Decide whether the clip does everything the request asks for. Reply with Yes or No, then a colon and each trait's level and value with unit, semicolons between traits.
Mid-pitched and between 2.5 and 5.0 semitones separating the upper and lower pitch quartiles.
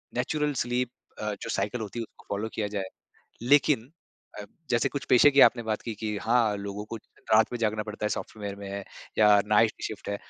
No: low, 110 Hz; average, 2.8 semitones